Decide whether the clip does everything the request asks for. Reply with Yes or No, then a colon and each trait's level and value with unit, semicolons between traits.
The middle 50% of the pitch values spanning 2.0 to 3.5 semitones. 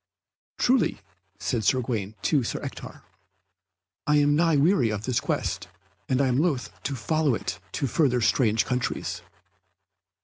No: average, 4.6 semitones